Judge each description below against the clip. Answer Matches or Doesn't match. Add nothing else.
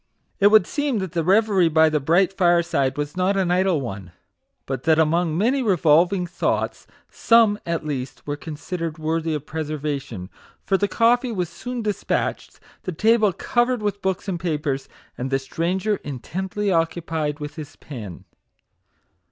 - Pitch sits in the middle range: Matches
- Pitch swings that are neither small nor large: Matches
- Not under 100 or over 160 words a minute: Matches